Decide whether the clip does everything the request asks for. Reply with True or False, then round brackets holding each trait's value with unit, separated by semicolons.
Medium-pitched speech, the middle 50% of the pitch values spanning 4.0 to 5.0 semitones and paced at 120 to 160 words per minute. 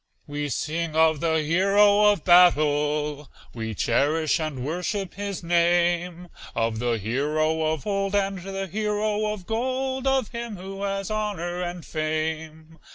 True (175 Hz; 4.5 semitones; 140 wpm)